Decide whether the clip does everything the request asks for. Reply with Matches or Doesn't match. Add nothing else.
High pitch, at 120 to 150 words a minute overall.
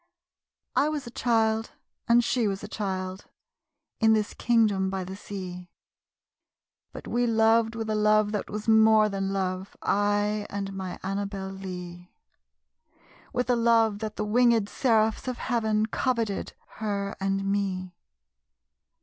Matches